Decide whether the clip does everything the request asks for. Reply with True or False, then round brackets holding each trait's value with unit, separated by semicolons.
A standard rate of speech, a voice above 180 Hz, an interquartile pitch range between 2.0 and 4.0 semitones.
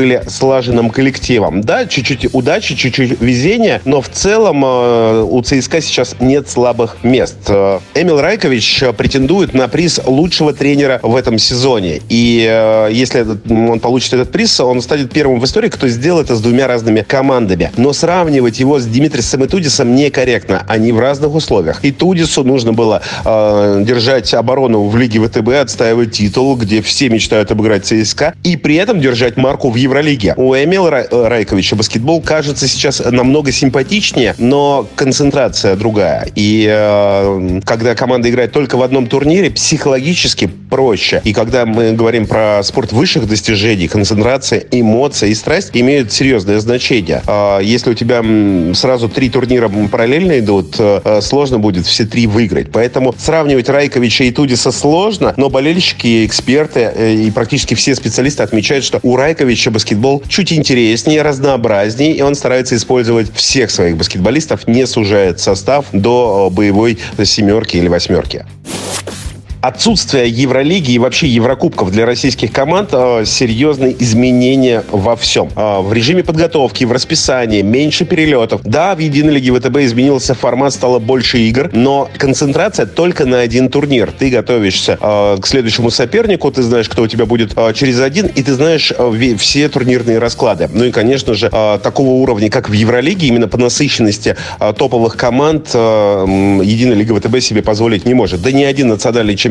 False (150 wpm; 125 Hz; 3.7 semitones)